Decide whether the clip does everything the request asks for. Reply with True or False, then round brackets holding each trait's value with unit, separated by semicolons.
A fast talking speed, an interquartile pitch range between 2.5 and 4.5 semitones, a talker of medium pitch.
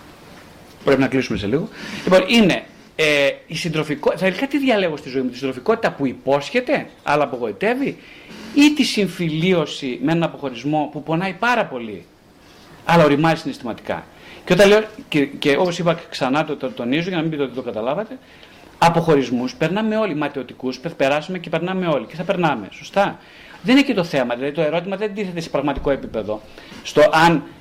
False (175 wpm; 5.4 semitones; 165 Hz)